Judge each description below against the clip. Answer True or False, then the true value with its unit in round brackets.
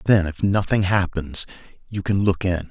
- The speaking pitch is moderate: False (95 Hz)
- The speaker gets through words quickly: False (175 wpm)